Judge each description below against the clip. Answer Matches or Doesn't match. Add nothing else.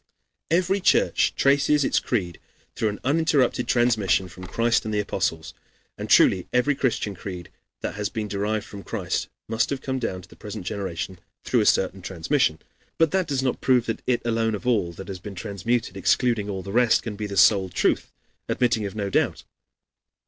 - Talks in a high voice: Doesn't match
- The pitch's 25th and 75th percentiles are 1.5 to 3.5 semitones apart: Doesn't match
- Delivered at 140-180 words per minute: Doesn't match